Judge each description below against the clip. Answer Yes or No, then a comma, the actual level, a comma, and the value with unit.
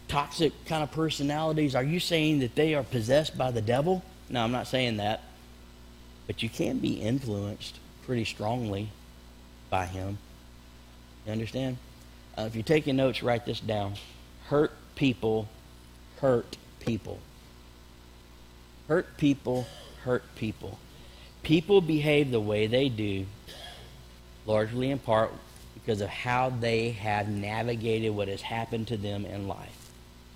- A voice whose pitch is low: Yes, low, 110 Hz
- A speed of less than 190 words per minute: Yes, slow, 135 wpm